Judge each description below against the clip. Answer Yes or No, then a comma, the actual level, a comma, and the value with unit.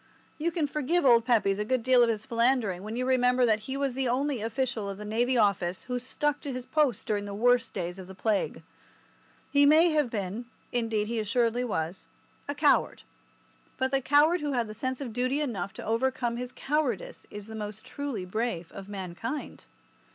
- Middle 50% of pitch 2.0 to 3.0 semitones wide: No, average, 4.1 semitones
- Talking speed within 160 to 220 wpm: Yes, average, 190 wpm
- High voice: Yes, high, 245 Hz